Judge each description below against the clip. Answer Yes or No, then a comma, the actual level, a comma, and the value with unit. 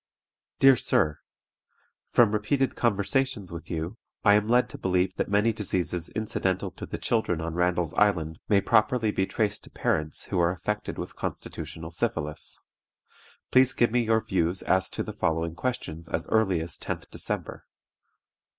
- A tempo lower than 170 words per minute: Yes, average, 160 wpm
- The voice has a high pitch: No, very low, 95 Hz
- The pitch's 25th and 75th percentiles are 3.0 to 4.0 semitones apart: No, average, 4.8 semitones